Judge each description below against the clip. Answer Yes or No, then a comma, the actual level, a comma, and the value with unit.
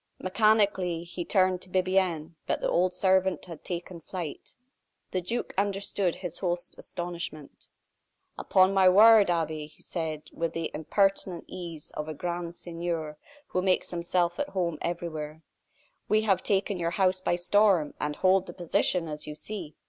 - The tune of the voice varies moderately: No, narrow, 2.3 semitones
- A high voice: No, medium, 175 Hz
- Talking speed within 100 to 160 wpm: Yes, average, 155 wpm